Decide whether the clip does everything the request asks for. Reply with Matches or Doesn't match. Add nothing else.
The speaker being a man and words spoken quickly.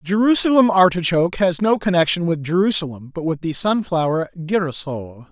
Doesn't match